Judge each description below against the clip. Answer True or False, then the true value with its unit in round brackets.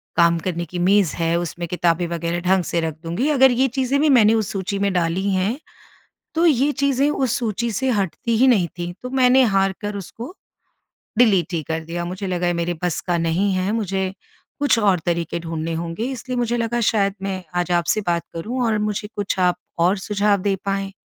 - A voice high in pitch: True (195 Hz)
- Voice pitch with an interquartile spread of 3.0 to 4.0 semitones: False (5.0 semitones)